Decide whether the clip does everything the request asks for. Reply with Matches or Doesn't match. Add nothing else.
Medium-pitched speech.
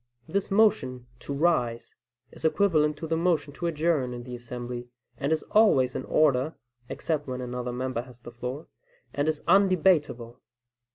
Matches